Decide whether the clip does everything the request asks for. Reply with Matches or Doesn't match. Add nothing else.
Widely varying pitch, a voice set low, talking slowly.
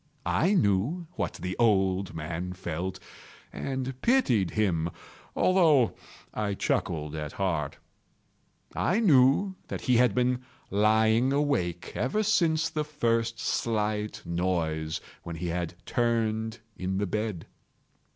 Matches